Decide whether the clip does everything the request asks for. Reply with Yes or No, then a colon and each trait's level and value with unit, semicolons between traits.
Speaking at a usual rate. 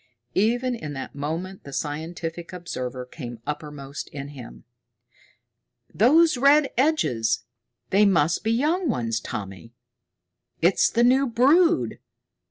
No: slow, 115 wpm